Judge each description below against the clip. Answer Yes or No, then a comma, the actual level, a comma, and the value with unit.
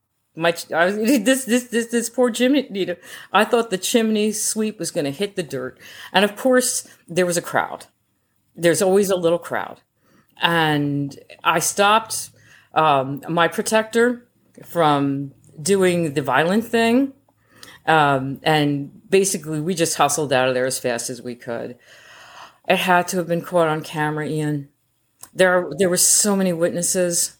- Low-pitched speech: No, medium, 170 Hz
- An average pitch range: No, wide, 6.1 semitones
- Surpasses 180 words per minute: No, average, 160 wpm